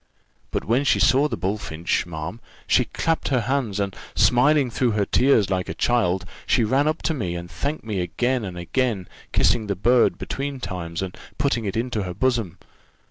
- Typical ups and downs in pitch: No, wide, 5.9 semitones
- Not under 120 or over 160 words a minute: No, average, 190 wpm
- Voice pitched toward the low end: Yes, low, 110 Hz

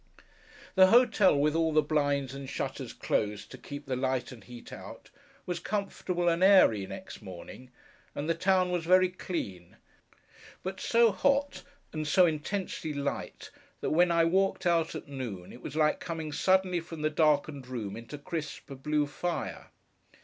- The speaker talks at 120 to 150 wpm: No, average, 165 wpm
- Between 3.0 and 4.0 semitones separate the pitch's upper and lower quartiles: No, average, 4.7 semitones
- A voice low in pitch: No, medium, 155 Hz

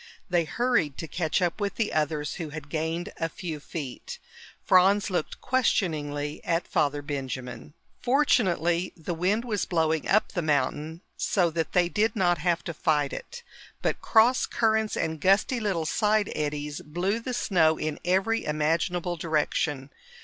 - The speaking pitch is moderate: Yes, medium, 170 Hz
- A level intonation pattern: No, average, 4.7 semitones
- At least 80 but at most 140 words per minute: No, average, 155 wpm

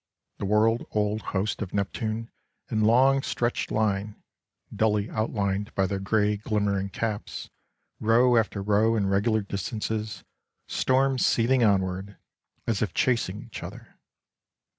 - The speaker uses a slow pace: Yes, slow, 125 wpm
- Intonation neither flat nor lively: No, narrow, 2.1 semitones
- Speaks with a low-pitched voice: Yes, low, 105 Hz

